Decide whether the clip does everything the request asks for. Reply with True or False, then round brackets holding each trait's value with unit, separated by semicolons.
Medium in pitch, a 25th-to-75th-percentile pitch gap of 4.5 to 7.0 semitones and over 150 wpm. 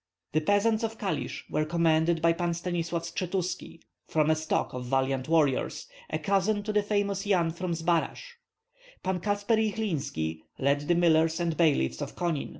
False (170 Hz; 3.9 semitones; 160 wpm)